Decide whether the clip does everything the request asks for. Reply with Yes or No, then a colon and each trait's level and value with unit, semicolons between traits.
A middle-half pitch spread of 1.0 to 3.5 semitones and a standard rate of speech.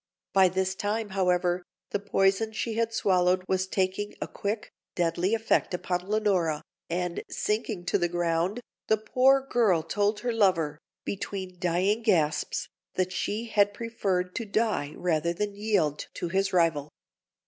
Yes: average, 3.1 semitones; average, 150 wpm